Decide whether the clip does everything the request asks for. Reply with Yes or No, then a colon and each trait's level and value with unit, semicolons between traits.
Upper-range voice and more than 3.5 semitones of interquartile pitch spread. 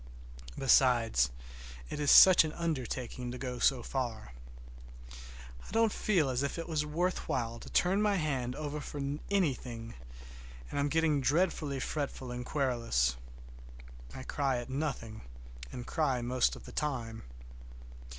No: low, 135 Hz; average, 4.0 semitones